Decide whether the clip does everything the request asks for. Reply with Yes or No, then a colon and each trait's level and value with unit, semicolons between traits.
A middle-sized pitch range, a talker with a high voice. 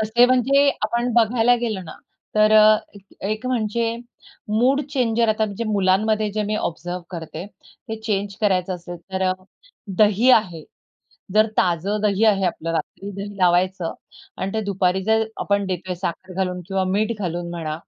Yes: average, 3.1 semitones; high, 205 Hz